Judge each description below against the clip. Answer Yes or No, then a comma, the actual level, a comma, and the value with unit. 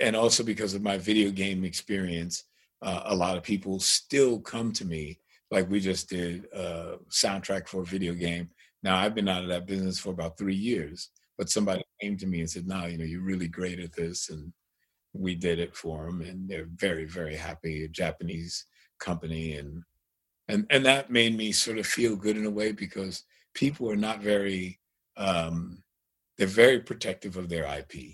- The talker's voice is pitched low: Yes, very low, 95 Hz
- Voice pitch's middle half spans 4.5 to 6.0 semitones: No, average, 3.1 semitones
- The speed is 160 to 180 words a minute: No, average, 200 wpm